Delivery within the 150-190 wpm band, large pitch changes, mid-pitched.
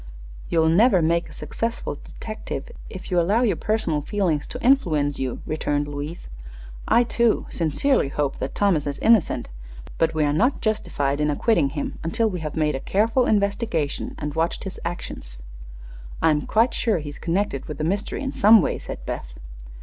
Yes: average, 175 wpm; wide, 6.6 semitones; medium, 170 Hz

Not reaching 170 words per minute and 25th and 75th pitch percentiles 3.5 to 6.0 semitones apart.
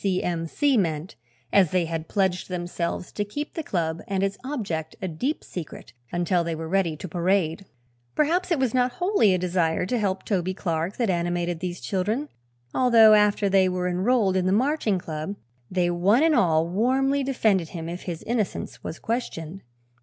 No: average, 185 wpm; average, 4.6 semitones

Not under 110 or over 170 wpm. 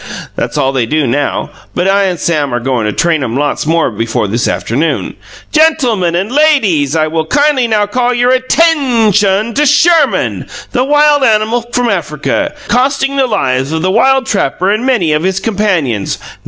No: average, 195 wpm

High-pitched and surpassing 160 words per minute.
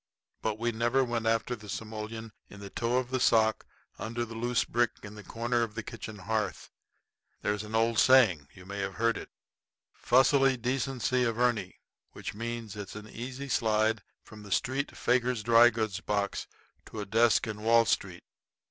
No: low, 115 Hz; average, 175 wpm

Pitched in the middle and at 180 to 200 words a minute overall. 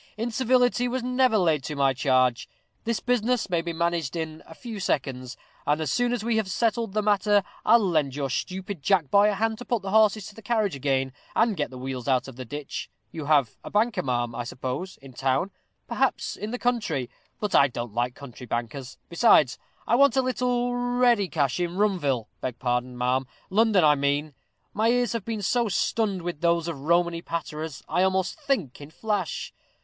Yes: medium, 175 Hz; average, 195 wpm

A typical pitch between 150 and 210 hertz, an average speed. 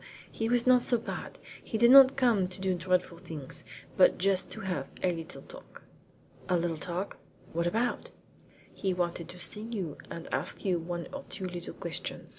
Yes: medium, 185 Hz; average, 185 wpm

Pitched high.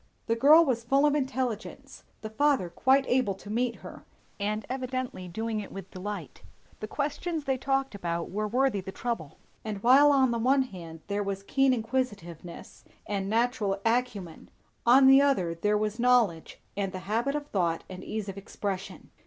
Yes: high, 225 Hz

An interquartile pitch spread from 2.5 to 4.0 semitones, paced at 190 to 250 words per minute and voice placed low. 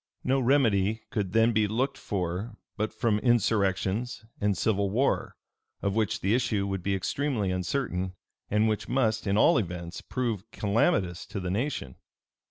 No: average, 3.3 semitones; average, 155 wpm; low, 105 Hz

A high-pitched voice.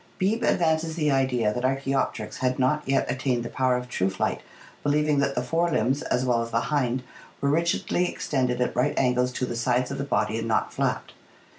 No: low, 130 Hz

